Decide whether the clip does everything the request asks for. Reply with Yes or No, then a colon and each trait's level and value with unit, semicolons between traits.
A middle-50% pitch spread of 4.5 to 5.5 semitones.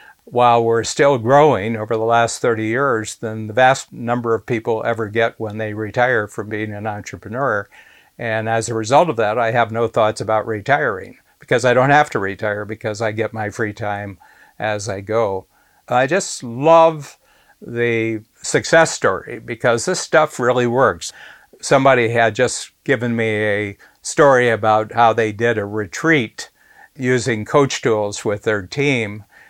No: average, 2.7 semitones